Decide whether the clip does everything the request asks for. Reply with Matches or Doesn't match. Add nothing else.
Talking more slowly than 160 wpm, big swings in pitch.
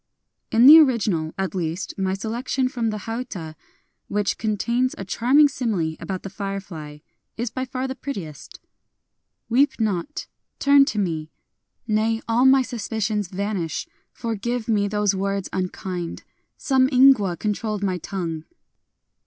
Doesn't match